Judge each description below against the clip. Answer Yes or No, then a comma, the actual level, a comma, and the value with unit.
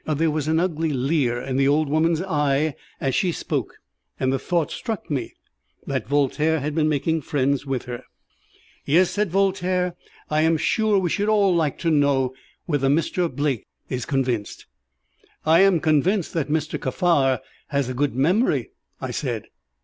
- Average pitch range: Yes, average, 3.9 semitones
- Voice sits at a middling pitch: Yes, medium, 155 Hz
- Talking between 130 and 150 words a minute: No, average, 165 wpm